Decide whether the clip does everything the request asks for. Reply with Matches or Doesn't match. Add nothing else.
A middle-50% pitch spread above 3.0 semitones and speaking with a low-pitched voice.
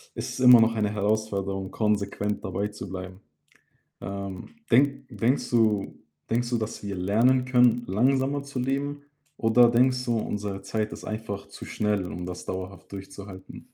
Matches